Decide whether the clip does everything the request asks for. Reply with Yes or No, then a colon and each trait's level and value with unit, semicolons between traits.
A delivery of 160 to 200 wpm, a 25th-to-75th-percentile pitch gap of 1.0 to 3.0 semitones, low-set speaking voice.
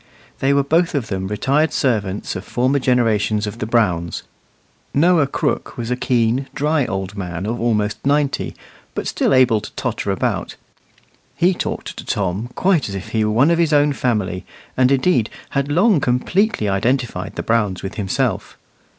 No: average, 170 wpm; average, 5.3 semitones; low, 120 Hz